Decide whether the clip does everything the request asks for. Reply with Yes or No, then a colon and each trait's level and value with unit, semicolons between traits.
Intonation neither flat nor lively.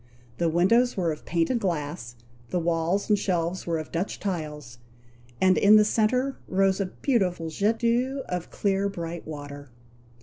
Yes: average, 4.2 semitones